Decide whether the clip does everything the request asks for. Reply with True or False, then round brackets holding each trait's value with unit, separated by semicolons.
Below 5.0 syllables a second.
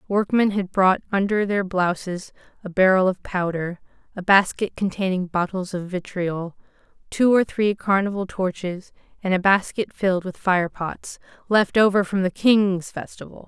True (4.5 syllables/s)